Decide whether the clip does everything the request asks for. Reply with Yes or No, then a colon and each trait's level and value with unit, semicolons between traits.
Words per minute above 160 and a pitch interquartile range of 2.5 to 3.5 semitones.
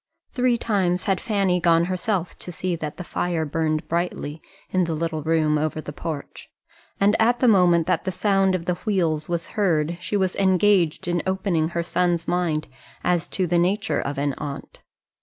Yes: average, 185 wpm; average, 2.8 semitones